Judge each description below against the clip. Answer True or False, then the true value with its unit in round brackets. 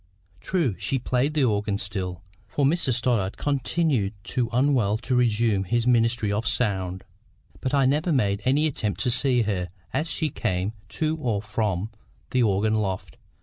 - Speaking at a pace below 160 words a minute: False (165 wpm)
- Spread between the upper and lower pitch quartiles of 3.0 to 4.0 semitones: False (4.6 semitones)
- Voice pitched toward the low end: True (115 Hz)